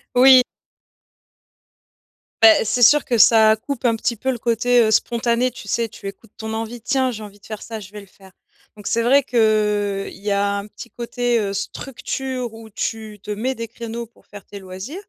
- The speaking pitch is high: Yes, high, 225 Hz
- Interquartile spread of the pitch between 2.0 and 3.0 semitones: Yes, narrow, 2.6 semitones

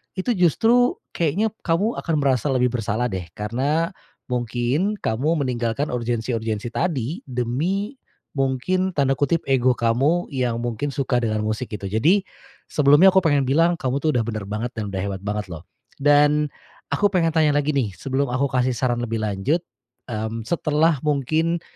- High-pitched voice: No, low, 135 Hz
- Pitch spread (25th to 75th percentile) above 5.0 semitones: Yes, wide, 5.6 semitones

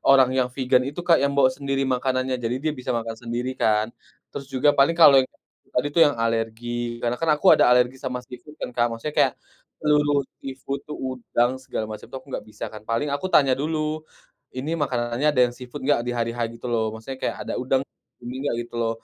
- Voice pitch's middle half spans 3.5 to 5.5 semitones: No, average, 2.7 semitones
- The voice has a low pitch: Yes, low, 130 Hz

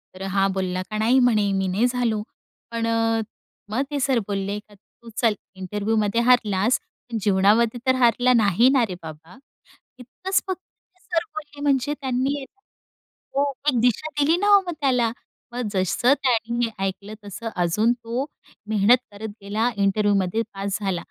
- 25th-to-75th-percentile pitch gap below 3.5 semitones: No, average, 4.0 semitones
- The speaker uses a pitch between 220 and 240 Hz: Yes, high, 225 Hz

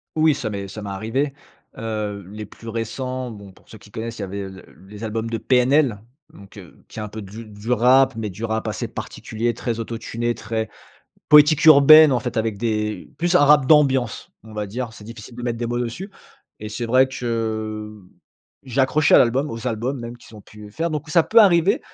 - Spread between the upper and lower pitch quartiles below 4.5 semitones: Yes, average, 3.5 semitones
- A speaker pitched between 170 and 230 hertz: No, low, 115 Hz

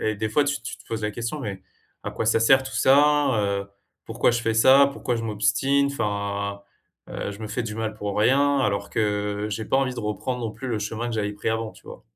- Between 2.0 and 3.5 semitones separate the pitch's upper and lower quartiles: No, average, 4.0 semitones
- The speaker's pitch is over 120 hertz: No, low, 110 Hz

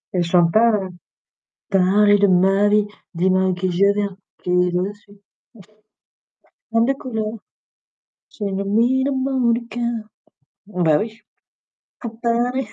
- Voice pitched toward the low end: No, high, 205 Hz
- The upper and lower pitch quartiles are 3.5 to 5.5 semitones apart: Yes, average, 3.8 semitones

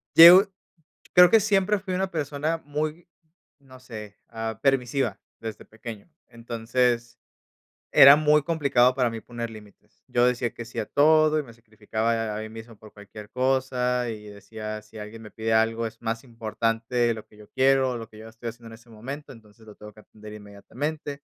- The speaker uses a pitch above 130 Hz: No, low, 115 Hz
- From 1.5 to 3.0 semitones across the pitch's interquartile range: No, average, 3.7 semitones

